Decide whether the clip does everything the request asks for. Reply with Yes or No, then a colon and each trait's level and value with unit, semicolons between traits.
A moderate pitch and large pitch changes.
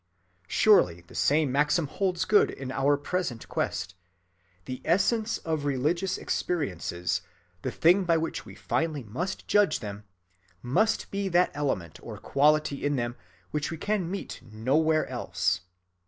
Yes: medium, 150 Hz; wide, 5.9 semitones